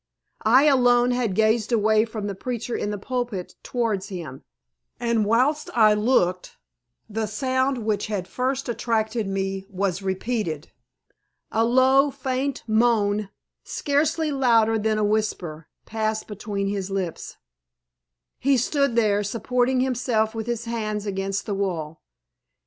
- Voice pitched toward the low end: No, high, 220 Hz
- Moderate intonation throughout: Yes, average, 3.5 semitones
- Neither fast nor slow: No, slow, 130 wpm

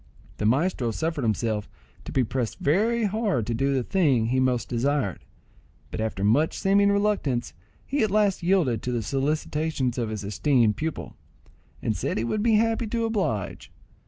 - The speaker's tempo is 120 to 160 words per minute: No, average, 175 wpm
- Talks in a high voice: No, medium, 140 Hz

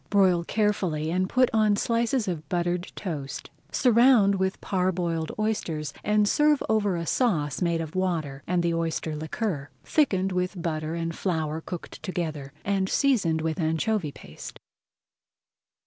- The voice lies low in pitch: No, medium, 180 Hz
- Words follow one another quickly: No, average, 140 wpm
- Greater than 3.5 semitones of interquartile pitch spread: Yes, average, 4.4 semitones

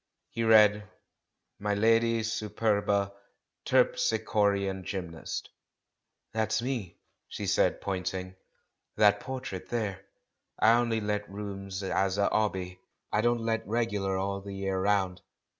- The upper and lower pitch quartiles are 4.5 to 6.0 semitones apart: No, narrow, 2.6 semitones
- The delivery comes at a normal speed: No, slow, 115 wpm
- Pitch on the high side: No, low, 105 Hz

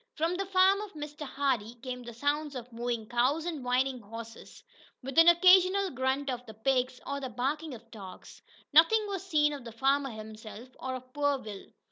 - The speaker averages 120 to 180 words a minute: No, average, 190 wpm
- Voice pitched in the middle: No, very high, 265 Hz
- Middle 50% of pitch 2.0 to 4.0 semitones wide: No, average, 4.4 semitones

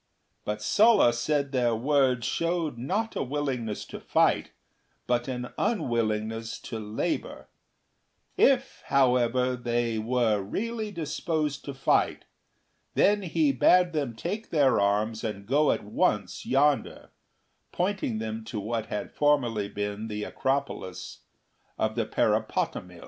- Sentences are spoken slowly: Yes, slow, 120 wpm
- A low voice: Yes, low, 125 Hz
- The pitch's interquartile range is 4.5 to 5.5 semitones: Yes, average, 5.1 semitones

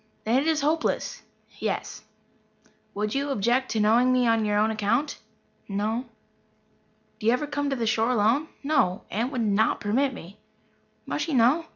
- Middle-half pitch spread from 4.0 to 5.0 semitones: Yes, average, 4.5 semitones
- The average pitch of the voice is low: No, high, 235 Hz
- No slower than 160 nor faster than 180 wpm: Yes, average, 170 wpm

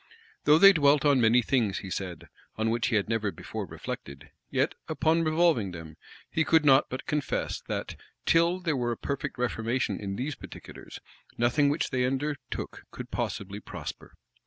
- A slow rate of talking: No, average, 170 wpm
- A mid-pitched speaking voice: No, low, 125 Hz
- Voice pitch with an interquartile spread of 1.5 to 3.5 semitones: No, average, 5.2 semitones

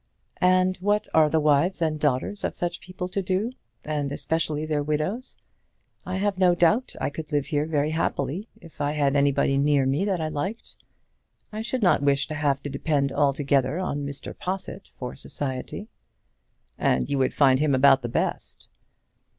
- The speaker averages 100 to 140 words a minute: No, average, 175 wpm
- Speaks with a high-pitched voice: No, medium, 150 Hz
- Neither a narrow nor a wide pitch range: Yes, average, 4.5 semitones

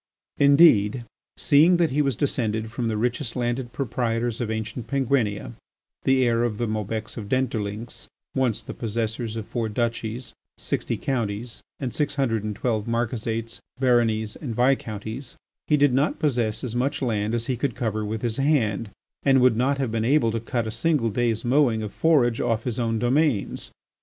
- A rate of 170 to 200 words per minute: Yes, average, 175 wpm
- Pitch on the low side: Yes, low, 120 Hz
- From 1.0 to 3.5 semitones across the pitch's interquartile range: Yes, average, 3.0 semitones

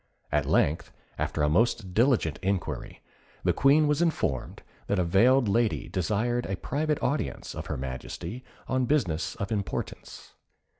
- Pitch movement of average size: No, wide, 7.1 semitones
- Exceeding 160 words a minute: No, average, 145 wpm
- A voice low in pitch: Yes, low, 105 Hz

